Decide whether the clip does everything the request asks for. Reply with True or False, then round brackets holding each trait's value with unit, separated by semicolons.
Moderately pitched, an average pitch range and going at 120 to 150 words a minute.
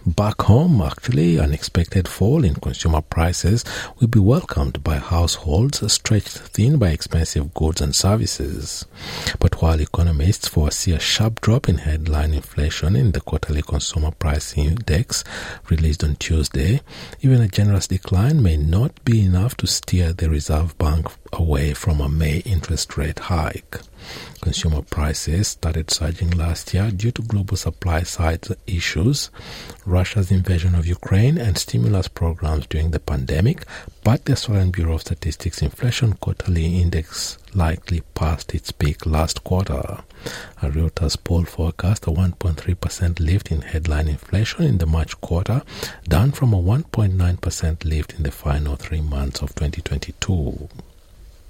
False (85 Hz; 4.2 semitones; 140 wpm)